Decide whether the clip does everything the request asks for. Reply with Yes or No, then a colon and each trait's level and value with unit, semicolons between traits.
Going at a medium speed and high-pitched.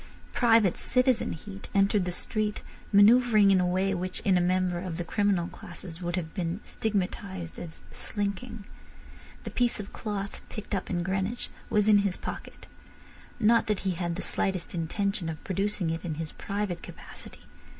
Yes: average, 170 wpm; high, 195 Hz